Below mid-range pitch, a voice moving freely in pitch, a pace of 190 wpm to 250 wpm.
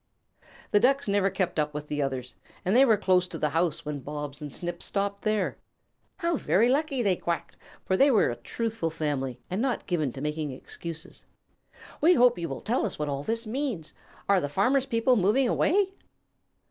No: medium, 185 Hz; wide, 7.6 semitones; average, 195 wpm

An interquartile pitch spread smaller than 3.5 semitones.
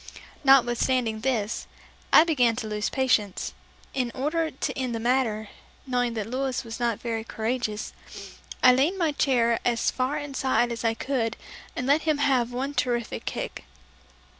Yes: average, 2.7 semitones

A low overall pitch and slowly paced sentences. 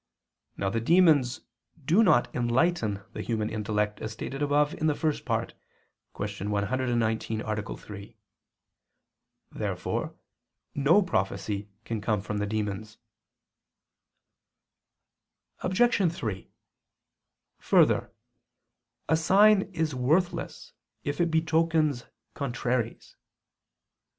Yes: low, 125 Hz; slow, 95 wpm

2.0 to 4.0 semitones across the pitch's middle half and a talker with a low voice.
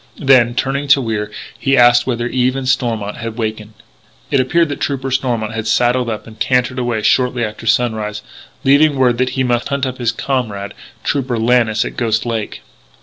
Yes: average, 2.7 semitones; low, 120 Hz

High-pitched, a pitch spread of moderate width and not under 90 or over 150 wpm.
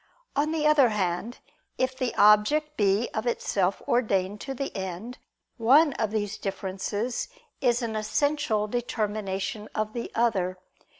Yes: high, 220 Hz; average, 3.9 semitones; slow, 135 wpm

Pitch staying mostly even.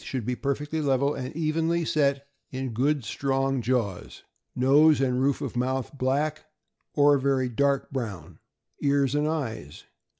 Yes: narrow, 2.3 semitones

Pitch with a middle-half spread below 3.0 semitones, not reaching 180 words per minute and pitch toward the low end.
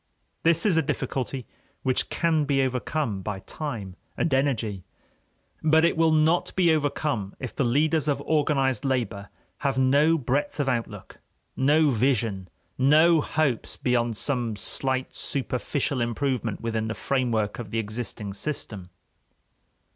No: average, 4.7 semitones; slow, 135 wpm; low, 130 Hz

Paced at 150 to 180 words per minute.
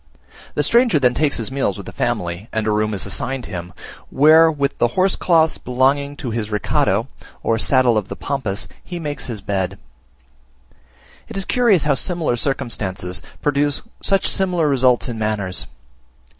Yes: average, 160 wpm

